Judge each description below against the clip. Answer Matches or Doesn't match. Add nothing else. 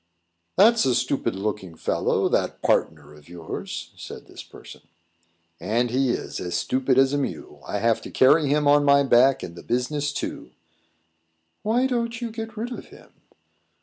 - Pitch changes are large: Matches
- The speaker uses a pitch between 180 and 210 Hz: Doesn't match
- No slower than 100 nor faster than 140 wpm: Doesn't match